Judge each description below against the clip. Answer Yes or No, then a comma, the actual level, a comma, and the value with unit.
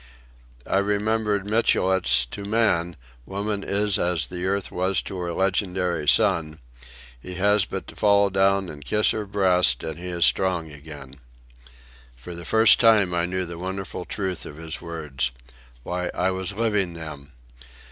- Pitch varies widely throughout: No, average, 3.0 semitones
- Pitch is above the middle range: No, very low, 95 Hz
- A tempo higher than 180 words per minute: No, average, 155 wpm